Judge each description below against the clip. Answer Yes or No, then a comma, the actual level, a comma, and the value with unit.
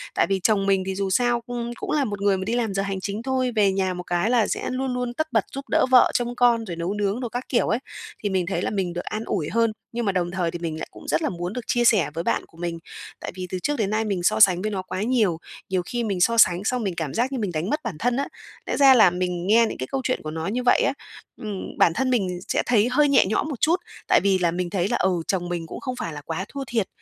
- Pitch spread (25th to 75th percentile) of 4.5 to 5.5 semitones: Yes, average, 5.1 semitones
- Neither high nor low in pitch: No, high, 200 Hz